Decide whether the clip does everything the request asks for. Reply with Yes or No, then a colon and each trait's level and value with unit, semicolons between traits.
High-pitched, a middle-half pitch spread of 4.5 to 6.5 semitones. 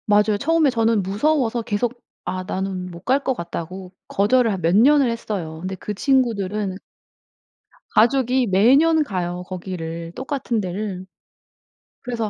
Yes: high, 210 Hz; average, 5.2 semitones